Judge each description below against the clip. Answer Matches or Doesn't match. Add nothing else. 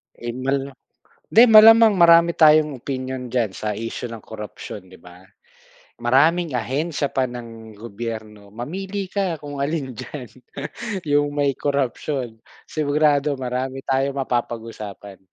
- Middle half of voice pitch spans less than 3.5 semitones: Doesn't match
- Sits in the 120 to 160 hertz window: Matches